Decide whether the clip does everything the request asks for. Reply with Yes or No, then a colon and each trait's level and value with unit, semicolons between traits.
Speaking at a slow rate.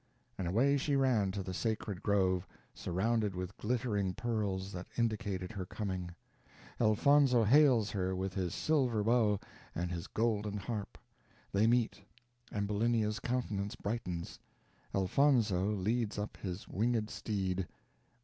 Yes: slow, 125 wpm